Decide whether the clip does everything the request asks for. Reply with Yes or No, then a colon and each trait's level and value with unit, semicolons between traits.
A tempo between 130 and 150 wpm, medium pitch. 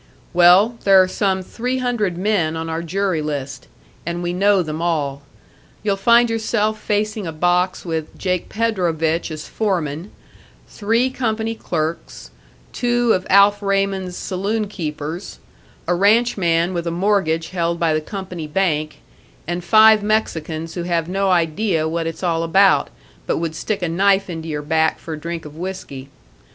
No: average, 160 wpm; medium, 180 Hz